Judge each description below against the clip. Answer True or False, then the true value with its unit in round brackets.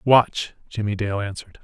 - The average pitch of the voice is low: True (105 Hz)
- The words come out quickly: False (145 wpm)